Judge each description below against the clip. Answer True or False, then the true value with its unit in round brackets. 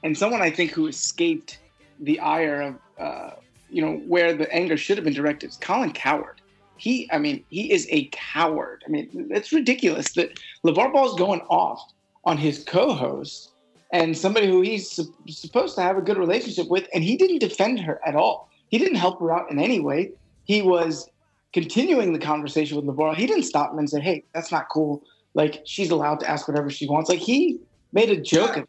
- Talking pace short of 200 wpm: False (205 wpm)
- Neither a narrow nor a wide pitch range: False (8.0 semitones)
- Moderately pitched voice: True (175 Hz)